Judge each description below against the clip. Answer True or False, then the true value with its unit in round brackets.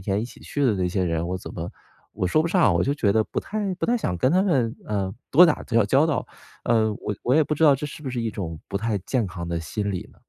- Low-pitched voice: True (115 Hz)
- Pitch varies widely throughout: True (7.7 semitones)